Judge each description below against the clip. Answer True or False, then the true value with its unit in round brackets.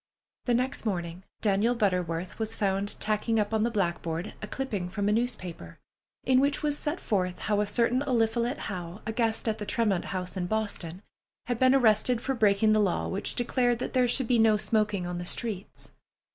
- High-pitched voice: True (215 Hz)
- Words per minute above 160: True (195 wpm)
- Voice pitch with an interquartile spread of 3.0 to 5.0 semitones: True (3.9 semitones)